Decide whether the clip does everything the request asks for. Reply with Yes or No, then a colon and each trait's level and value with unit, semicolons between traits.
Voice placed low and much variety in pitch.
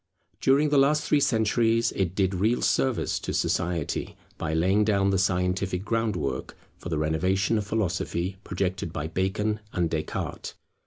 No: very low, 95 Hz; average, 4.0 semitones